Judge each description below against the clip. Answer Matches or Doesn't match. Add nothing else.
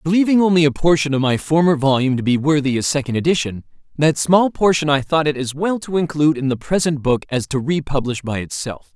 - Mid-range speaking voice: Matches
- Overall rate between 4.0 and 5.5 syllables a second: Doesn't match